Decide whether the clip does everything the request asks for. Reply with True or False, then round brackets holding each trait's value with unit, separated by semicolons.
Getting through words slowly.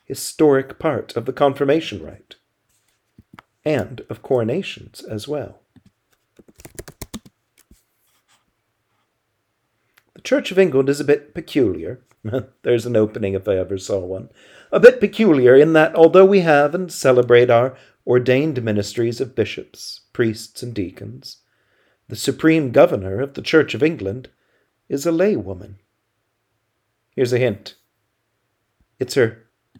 True (125 wpm)